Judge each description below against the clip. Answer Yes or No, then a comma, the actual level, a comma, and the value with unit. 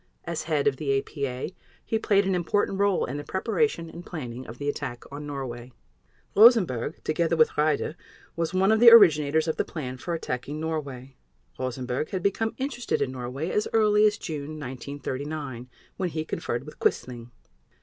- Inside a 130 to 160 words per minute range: No, average, 170 wpm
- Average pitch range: No, wide, 6.1 semitones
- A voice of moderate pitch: Yes, medium, 155 Hz